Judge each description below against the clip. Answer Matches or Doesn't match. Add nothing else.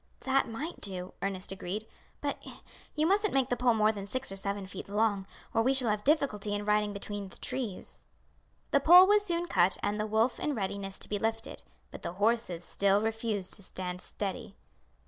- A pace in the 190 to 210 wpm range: Matches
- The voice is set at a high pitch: Matches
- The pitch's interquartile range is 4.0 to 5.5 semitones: Matches